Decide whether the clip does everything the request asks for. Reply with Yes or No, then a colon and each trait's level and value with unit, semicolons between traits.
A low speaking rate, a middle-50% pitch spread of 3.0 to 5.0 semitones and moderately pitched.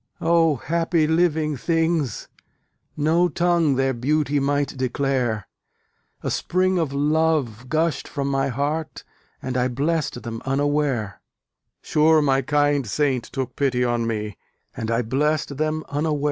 Yes: slow, 130 wpm; average, 3.5 semitones; medium, 145 Hz